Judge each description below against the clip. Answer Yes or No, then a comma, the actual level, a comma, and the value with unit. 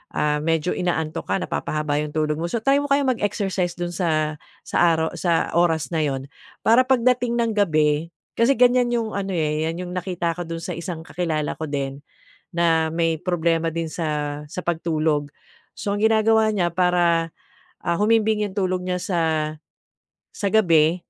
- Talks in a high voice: No, medium, 170 Hz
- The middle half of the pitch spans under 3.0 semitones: No, average, 4.3 semitones